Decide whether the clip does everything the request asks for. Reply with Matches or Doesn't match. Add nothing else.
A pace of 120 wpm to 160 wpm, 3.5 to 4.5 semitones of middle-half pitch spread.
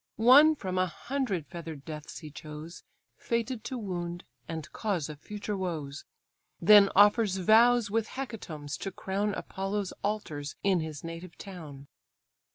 Doesn't match